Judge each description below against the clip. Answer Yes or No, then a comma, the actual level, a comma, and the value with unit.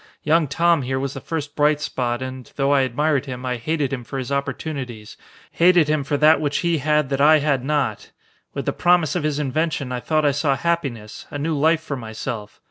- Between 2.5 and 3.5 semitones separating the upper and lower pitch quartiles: Yes, average, 3.0 semitones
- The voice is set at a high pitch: No, medium, 145 Hz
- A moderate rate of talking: No, fast, 215 wpm